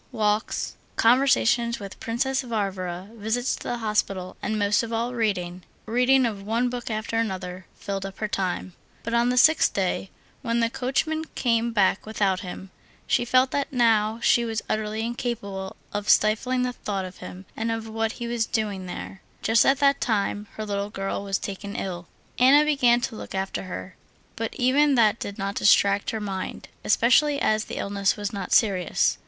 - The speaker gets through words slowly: No, average, 175 wpm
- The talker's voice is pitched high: Yes, high, 220 Hz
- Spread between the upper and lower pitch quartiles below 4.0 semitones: Yes, average, 3.3 semitones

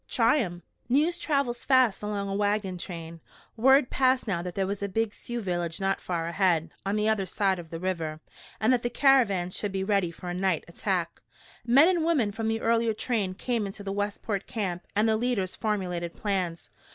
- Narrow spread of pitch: No, average, 4.2 semitones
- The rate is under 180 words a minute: No, average, 200 wpm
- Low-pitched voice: No, high, 200 Hz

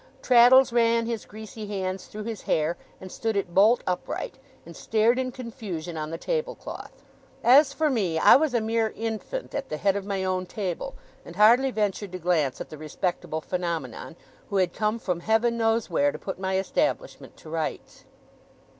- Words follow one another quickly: No, average, 185 wpm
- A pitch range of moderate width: Yes, average, 4.5 semitones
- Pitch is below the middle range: No, high, 210 Hz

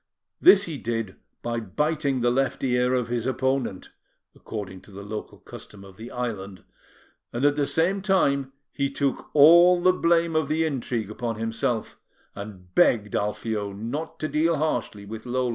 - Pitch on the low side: Yes, low, 125 Hz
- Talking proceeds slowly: No, average, 165 wpm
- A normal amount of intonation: No, wide, 5.8 semitones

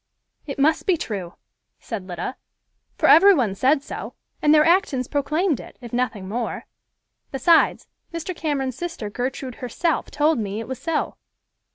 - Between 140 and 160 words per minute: Yes, average, 155 wpm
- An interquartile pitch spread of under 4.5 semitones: No, average, 5.3 semitones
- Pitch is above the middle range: Yes, very high, 270 Hz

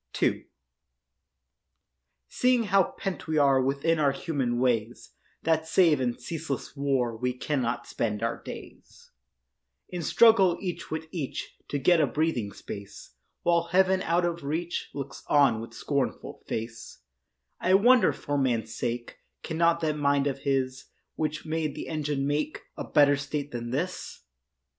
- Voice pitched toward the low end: No, medium, 145 Hz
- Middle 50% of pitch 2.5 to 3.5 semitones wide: No, average, 4.4 semitones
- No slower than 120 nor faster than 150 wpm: Yes, average, 145 wpm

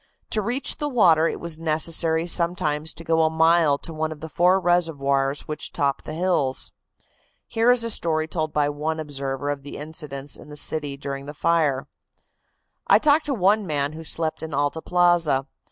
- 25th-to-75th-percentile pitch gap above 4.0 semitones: No, average, 3.0 semitones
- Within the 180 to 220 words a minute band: Yes, average, 185 wpm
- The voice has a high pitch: No, medium, 160 Hz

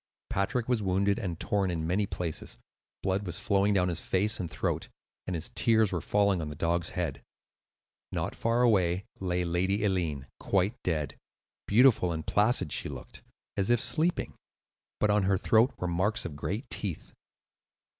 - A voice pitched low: Yes, very low, 95 Hz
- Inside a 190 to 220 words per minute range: No, average, 170 wpm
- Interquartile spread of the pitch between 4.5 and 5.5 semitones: No, average, 3.3 semitones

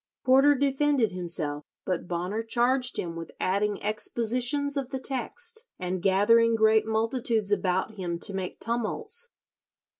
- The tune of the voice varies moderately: No, wide, 5.7 semitones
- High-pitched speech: Yes, high, 225 Hz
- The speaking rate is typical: No, slow, 130 wpm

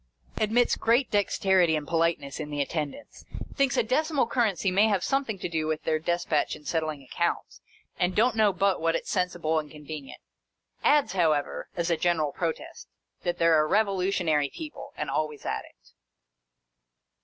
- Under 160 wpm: No, average, 175 wpm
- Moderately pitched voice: Yes, medium, 175 Hz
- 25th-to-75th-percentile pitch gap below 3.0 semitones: No, average, 5.0 semitones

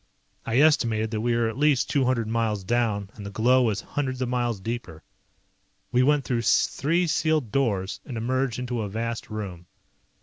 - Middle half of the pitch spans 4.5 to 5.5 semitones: No, average, 3.1 semitones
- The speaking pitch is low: Yes, low, 120 Hz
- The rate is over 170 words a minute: Yes, average, 180 wpm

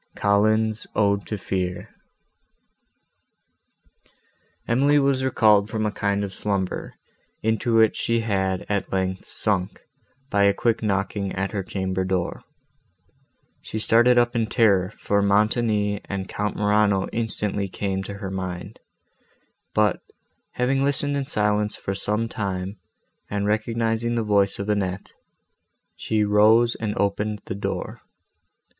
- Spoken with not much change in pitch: Yes, narrow, 2.3 semitones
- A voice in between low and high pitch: No, low, 105 Hz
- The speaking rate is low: Yes, slow, 130 wpm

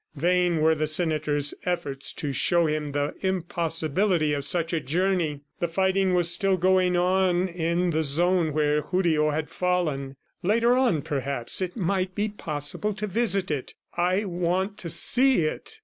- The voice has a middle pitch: Yes, medium, 175 Hz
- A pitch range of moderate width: Yes, average, 3.5 semitones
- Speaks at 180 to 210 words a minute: No, average, 160 wpm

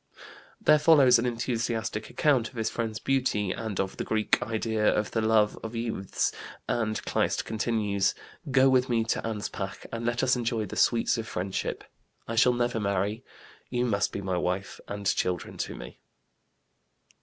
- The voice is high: No, low, 110 Hz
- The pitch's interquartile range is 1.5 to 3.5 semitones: Yes, average, 2.7 semitones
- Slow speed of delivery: No, average, 165 wpm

